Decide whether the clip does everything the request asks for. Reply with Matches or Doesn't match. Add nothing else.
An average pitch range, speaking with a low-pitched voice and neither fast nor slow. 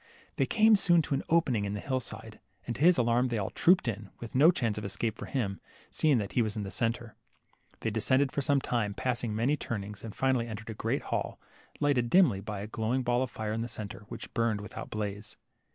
Doesn't match